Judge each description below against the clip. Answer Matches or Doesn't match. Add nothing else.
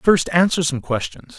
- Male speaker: Matches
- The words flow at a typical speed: Matches